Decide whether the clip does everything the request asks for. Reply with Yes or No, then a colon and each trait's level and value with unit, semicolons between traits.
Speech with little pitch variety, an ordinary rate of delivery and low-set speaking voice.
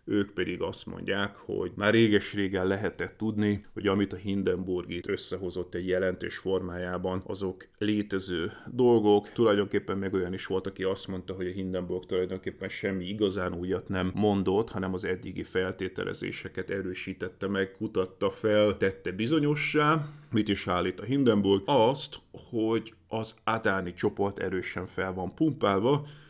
Yes: narrow, 2.3 semitones; average, 145 wpm; very low, 95 Hz